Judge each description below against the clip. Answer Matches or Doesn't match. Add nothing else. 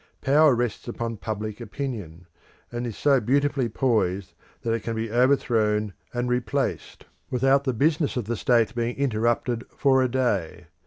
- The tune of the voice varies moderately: Matches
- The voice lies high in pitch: Doesn't match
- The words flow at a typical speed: Matches